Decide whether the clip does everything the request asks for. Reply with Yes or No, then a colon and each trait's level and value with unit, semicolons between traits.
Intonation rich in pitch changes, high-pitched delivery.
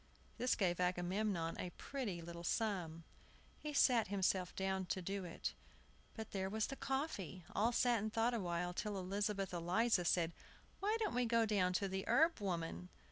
No: average, 4.1 semitones; high, 195 Hz